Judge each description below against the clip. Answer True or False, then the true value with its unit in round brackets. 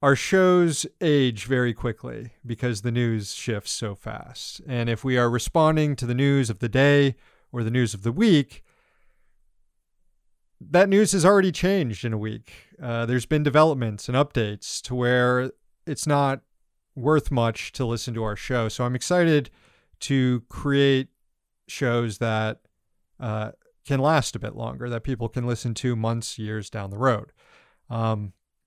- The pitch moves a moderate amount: True (3.8 semitones)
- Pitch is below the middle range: True (125 Hz)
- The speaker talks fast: False (160 wpm)